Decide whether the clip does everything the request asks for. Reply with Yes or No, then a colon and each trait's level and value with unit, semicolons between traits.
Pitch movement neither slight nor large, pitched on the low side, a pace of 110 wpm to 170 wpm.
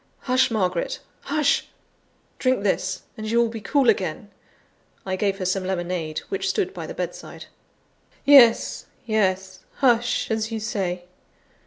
No: average, 4.4 semitones; high, 215 Hz; average, 140 wpm